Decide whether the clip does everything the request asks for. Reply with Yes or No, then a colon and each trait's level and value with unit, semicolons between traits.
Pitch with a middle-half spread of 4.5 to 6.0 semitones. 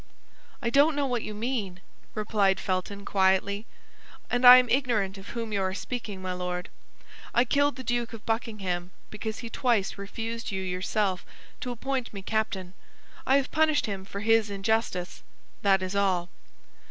No: average, 3.9 semitones